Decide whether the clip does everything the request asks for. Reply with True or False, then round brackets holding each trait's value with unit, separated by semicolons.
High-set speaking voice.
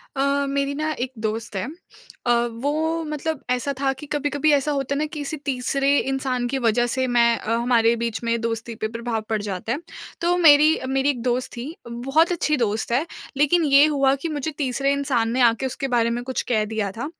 True (260 Hz)